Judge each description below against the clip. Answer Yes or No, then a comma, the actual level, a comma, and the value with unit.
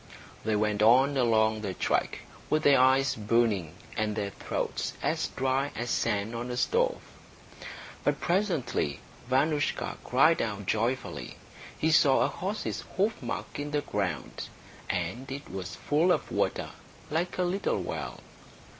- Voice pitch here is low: Yes, low, 130 Hz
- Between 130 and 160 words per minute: Yes, average, 140 wpm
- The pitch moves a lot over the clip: Yes, wide, 5.7 semitones